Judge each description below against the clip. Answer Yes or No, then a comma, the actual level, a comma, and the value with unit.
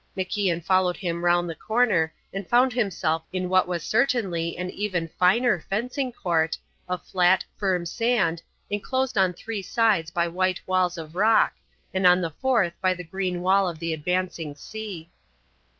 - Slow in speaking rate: No, average, 165 wpm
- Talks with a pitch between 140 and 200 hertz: Yes, medium, 185 Hz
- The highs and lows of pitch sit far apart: No, average, 3.4 semitones